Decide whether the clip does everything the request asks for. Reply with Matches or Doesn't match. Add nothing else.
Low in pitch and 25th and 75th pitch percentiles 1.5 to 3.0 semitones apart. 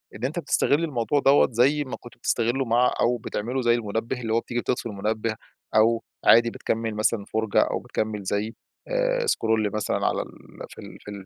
Matches